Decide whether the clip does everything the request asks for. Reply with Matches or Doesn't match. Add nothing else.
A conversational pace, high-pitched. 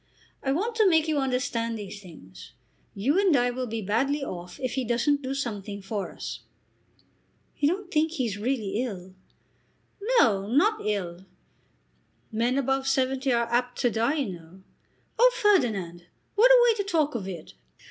Matches